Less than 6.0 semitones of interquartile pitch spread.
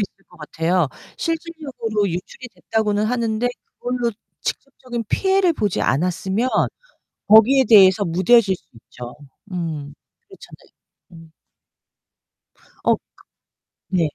Yes: wide, 5.6 semitones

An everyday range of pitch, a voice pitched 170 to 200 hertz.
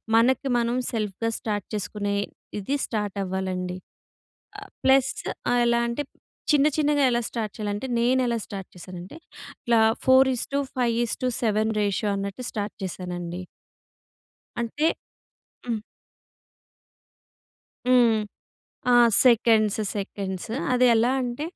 No: average, 3.7 semitones; high, 225 Hz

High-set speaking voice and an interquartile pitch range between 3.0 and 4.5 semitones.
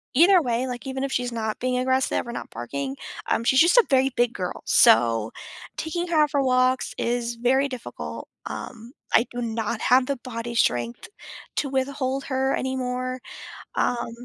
No: very high, 255 Hz; narrow, 2.4 semitones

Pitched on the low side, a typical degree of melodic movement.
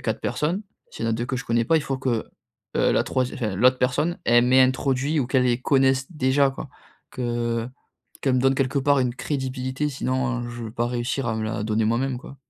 No: low, 130 Hz; narrow, 2.1 semitones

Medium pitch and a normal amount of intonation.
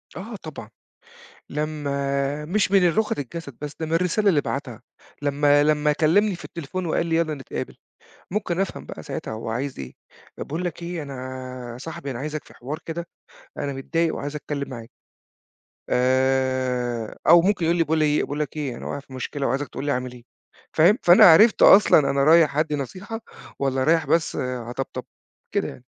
Yes: medium, 150 Hz; average, 3.8 semitones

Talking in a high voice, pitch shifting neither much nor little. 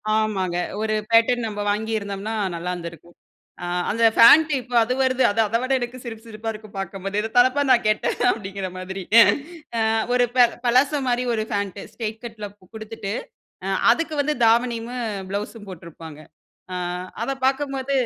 Yes: high, 220 Hz; average, 3.6 semitones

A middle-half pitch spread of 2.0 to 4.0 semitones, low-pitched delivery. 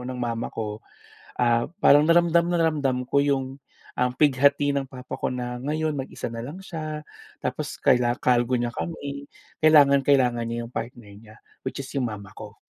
Yes: average, 3.3 semitones; low, 130 Hz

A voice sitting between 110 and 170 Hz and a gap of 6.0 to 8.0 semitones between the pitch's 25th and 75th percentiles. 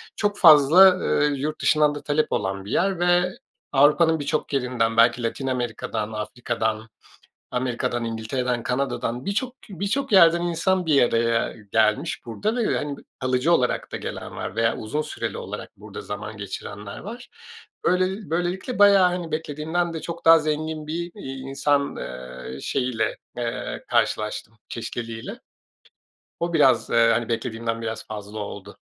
Yes: low, 135 Hz; wide, 6.8 semitones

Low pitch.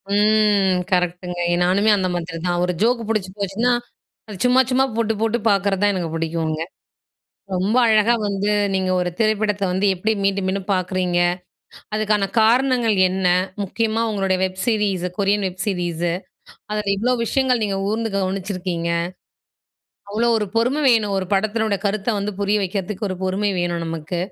No: high, 200 Hz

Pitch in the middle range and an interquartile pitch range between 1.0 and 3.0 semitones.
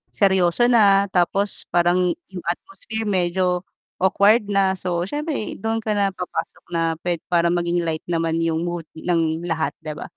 Yes: medium, 180 Hz; narrow, 2.6 semitones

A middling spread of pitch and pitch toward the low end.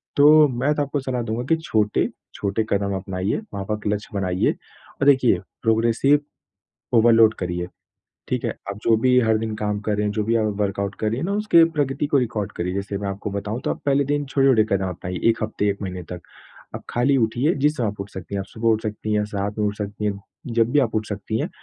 Yes: average, 4.0 semitones; low, 110 Hz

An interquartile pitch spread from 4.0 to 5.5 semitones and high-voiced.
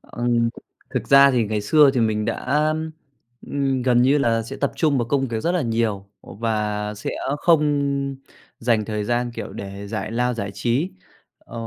No: average, 4.3 semitones; low, 120 Hz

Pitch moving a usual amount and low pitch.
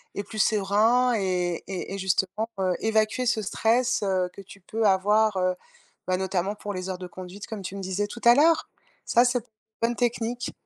No: average, 3.2 semitones; high, 205 Hz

